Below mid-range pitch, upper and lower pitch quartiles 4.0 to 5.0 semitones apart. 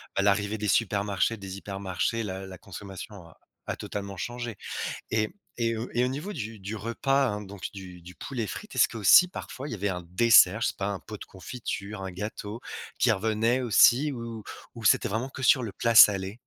No: low, 105 Hz; average, 3.1 semitones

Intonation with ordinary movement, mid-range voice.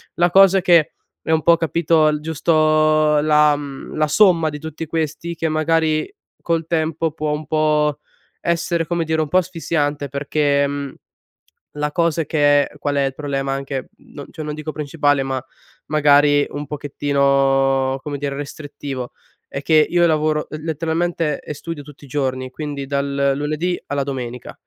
No: narrow, 2.1 semitones; medium, 150 Hz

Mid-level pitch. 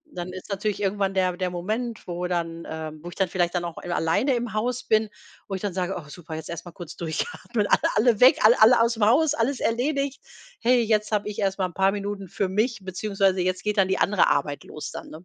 No: high, 195 Hz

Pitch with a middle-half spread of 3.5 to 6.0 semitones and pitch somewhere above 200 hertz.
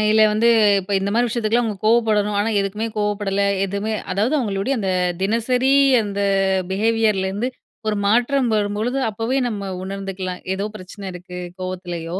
No: narrow, 2.6 semitones; high, 210 Hz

